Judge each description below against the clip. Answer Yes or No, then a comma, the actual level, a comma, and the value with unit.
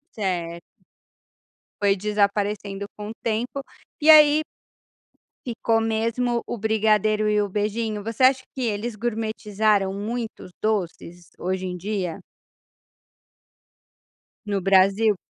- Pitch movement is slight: Yes, narrow, 2.3 semitones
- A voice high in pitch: Yes, high, 210 Hz